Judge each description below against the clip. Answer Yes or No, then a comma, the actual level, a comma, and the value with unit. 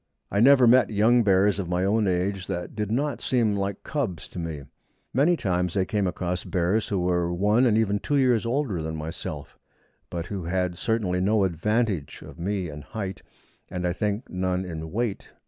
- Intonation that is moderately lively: Yes, average, 3.9 semitones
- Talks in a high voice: No, low, 100 Hz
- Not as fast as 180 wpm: No, average, 190 wpm